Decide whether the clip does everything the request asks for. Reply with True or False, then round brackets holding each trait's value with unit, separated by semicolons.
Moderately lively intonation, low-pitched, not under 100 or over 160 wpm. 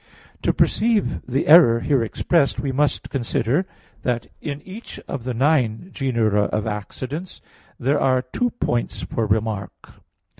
True (4.7 semitones; 130 Hz; 140 wpm)